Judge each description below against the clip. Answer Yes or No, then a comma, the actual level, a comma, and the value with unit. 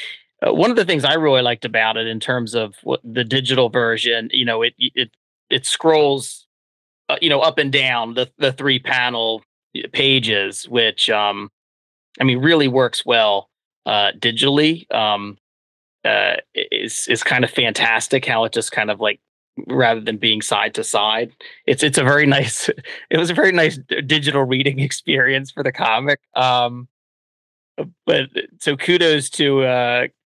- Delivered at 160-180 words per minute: Yes, average, 165 wpm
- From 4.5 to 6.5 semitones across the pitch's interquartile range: No, average, 3.7 semitones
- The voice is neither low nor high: No, low, 125 Hz